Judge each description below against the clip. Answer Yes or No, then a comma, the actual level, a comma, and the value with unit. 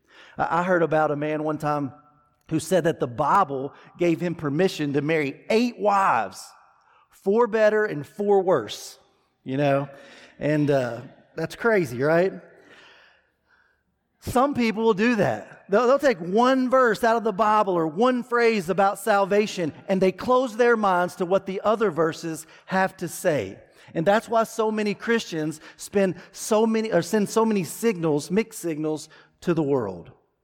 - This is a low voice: No, high, 190 Hz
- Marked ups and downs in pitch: Yes, wide, 5.9 semitones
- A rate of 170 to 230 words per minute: No, average, 160 wpm